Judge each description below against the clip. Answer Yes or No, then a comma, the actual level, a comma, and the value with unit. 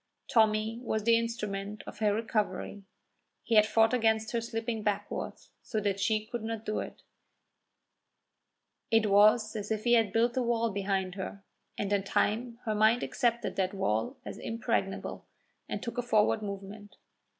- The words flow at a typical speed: Yes, average, 160 wpm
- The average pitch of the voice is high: Yes, high, 215 Hz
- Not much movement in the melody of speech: Yes, narrow, 2.0 semitones